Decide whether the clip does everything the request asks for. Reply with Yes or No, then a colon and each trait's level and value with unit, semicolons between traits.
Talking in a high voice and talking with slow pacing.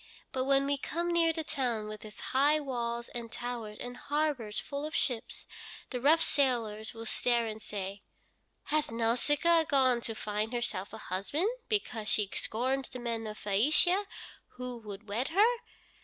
No: high, 245 Hz; average, 165 wpm